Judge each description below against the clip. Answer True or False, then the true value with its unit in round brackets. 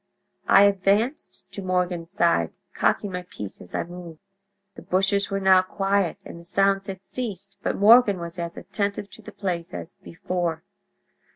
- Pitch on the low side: False (190 Hz)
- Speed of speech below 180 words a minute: True (165 wpm)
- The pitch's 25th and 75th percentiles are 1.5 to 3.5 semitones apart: True (2.6 semitones)